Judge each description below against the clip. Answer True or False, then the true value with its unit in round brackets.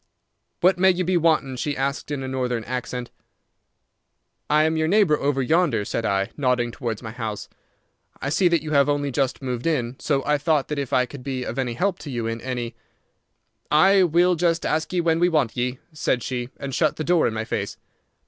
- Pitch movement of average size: True (4.5 semitones)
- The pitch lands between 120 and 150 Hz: True (140 Hz)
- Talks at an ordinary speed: False (215 wpm)